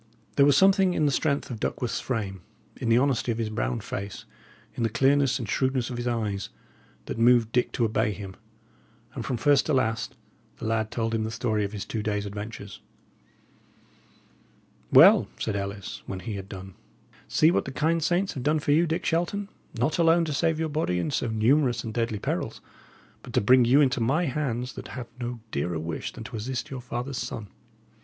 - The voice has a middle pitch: No, low, 120 Hz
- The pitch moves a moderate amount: Yes, average, 4.7 semitones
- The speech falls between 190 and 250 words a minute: Yes, average, 200 wpm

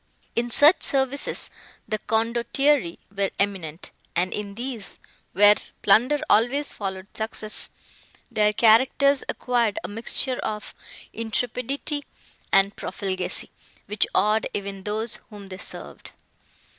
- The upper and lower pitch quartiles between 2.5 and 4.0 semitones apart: Yes, average, 3.7 semitones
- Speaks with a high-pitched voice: Yes, high, 215 Hz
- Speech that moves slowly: Yes, slow, 110 wpm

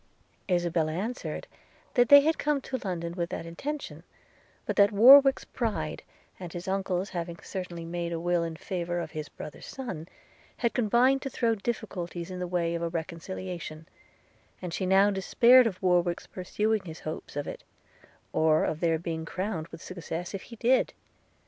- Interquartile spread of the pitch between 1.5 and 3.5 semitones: No, average, 4.5 semitones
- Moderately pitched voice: Yes, medium, 180 Hz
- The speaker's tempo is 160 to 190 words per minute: Yes, average, 170 wpm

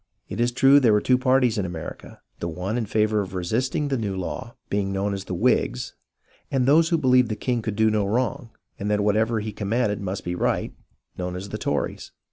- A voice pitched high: No, low, 110 Hz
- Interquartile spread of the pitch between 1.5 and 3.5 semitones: No, average, 4.1 semitones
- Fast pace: Yes, fast, 225 wpm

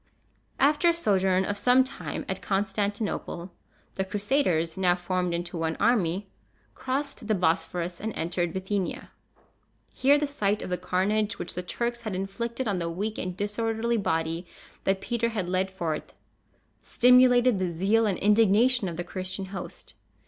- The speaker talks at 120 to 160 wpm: Yes, average, 155 wpm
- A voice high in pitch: Yes, high, 195 Hz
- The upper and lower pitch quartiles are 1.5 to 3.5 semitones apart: No, average, 4.2 semitones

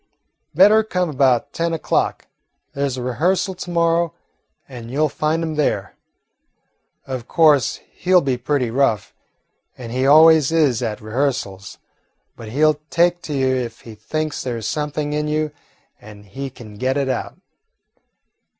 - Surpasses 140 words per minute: Yes, average, 160 wpm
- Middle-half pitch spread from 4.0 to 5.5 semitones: Yes, average, 4.4 semitones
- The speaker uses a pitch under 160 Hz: Yes, medium, 140 Hz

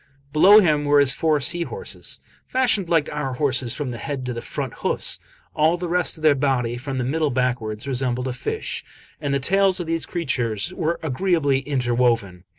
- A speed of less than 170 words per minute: No, average, 195 wpm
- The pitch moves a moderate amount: Yes, average, 4.7 semitones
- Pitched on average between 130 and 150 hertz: Yes, medium, 140 Hz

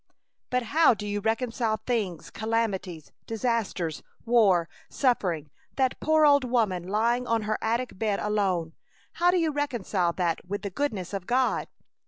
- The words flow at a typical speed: Yes, average, 150 wpm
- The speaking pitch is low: No, high, 220 Hz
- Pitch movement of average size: Yes, average, 4.7 semitones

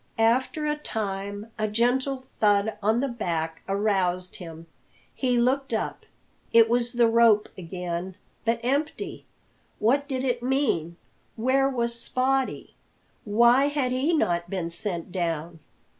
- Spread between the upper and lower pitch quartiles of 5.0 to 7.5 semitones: Yes, wide, 5.4 semitones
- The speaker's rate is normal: No, slow, 130 wpm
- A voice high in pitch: Yes, high, 230 Hz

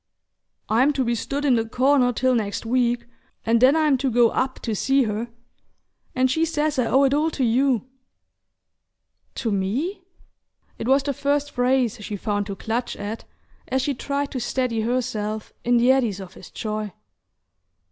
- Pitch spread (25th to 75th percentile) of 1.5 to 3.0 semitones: No, average, 3.4 semitones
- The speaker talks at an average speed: Yes, average, 175 wpm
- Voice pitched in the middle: No, very high, 250 Hz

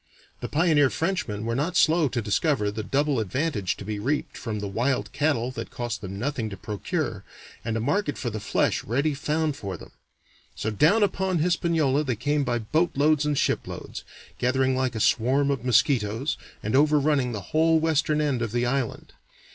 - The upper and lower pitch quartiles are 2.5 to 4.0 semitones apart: No, average, 5.1 semitones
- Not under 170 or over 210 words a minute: Yes, average, 180 wpm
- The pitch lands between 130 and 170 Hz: Yes, low, 135 Hz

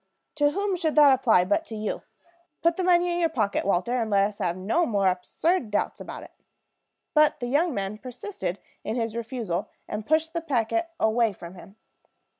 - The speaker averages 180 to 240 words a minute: Yes, average, 195 wpm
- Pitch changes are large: Yes, wide, 7.9 semitones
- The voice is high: Yes, high, 240 Hz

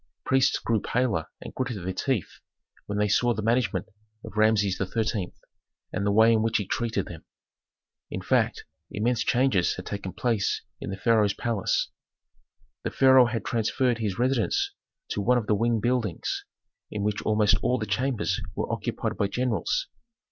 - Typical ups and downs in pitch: Yes, average, 3.2 semitones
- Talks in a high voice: No, low, 110 Hz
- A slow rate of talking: No, average, 165 wpm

